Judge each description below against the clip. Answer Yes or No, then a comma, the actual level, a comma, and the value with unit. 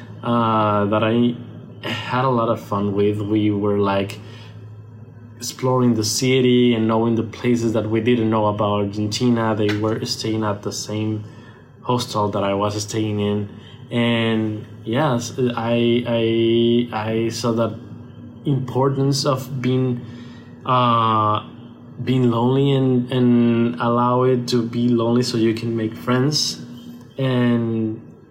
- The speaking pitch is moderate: No, low, 115 Hz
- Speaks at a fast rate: No, slow, 135 wpm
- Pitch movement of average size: No, narrow, 1.9 semitones